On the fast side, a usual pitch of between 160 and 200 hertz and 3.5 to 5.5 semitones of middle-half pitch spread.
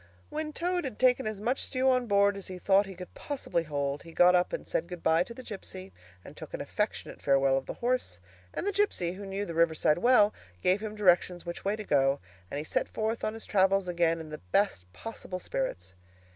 Yes: fast, 225 wpm; high, 190 Hz; average, 5.2 semitones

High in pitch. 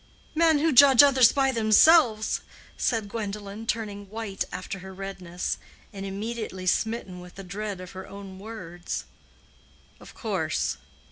Yes: high, 205 Hz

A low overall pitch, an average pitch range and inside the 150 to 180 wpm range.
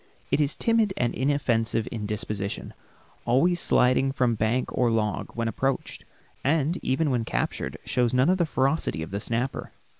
Yes: low, 125 Hz; average, 4.1 semitones; average, 160 wpm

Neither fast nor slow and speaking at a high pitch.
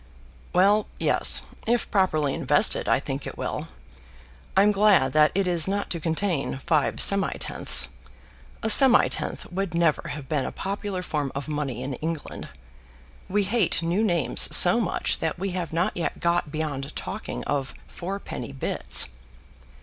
No: average, 150 wpm; medium, 170 Hz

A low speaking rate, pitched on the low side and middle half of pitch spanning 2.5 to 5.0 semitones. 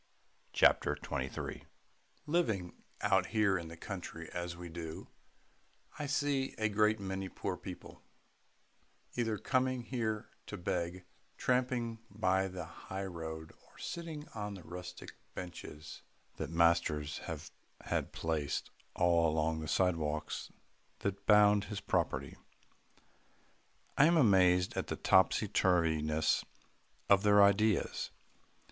Yes: slow, 125 wpm; very low, 95 Hz; average, 4.4 semitones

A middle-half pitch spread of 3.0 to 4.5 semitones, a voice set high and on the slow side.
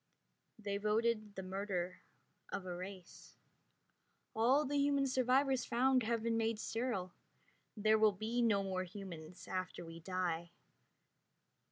Yes: average, 4.1 semitones; high, 210 Hz; slow, 130 wpm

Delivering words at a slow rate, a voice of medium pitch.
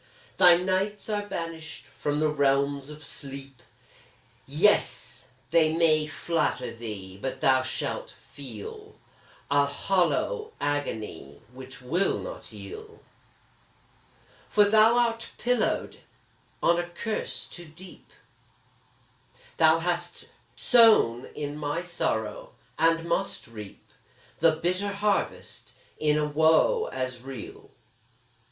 Yes: slow, 105 wpm; medium, 160 Hz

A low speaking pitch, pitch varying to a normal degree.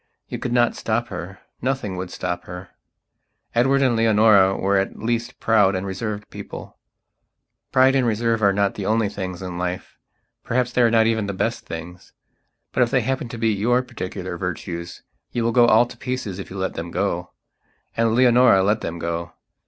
Yes: low, 105 Hz; average, 4.2 semitones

